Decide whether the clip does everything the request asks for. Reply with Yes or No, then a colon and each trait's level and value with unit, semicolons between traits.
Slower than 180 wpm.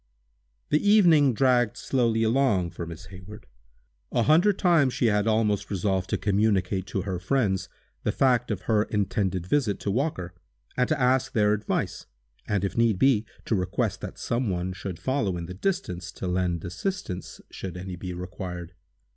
Yes: average, 170 wpm